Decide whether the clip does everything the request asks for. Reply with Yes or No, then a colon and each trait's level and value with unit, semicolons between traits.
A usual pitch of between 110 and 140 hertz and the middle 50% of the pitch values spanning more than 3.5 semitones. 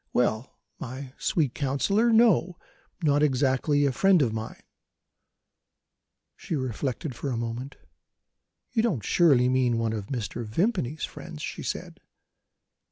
Yes: low, 135 Hz; average, 5.0 semitones